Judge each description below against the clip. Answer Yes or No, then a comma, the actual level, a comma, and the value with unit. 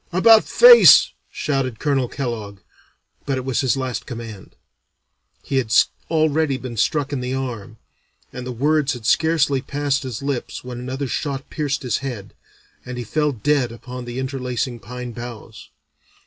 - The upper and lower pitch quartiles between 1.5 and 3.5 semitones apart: Yes, average, 2.8 semitones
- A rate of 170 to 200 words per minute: No, average, 155 wpm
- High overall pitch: No, low, 130 Hz